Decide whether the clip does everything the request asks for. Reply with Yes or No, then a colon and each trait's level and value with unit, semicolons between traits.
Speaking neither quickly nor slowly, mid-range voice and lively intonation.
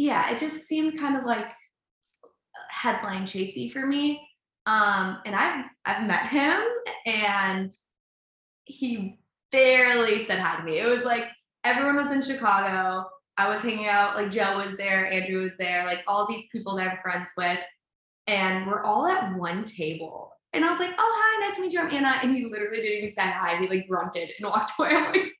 No: average, 195 wpm; high, 210 Hz; wide, 6.3 semitones